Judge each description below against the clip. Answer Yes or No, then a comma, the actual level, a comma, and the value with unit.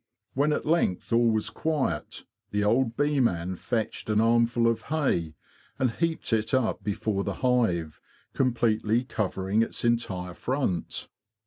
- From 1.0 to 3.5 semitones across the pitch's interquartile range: No, average, 3.9 semitones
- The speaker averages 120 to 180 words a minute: Yes, average, 140 wpm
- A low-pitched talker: Yes, low, 115 Hz